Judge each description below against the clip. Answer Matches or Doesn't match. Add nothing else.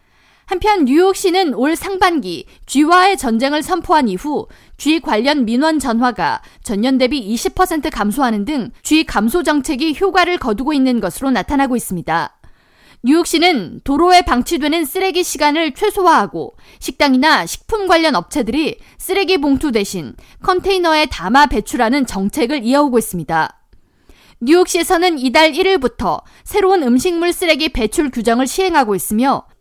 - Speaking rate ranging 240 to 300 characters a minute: Doesn't match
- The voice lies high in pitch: Matches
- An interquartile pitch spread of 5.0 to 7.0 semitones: Matches